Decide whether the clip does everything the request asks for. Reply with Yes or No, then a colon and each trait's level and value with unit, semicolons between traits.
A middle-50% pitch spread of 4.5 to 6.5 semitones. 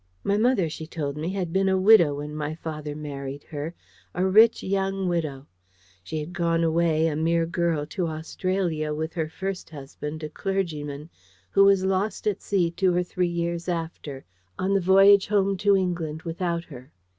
No: average, 3.6 semitones